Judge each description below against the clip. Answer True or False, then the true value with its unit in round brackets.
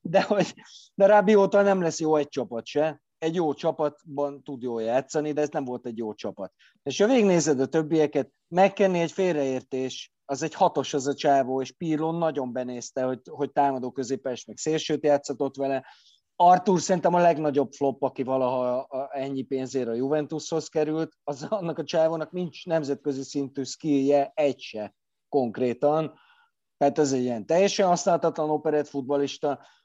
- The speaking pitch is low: False (145 Hz)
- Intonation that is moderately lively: True (3.3 semitones)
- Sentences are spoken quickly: True (160 wpm)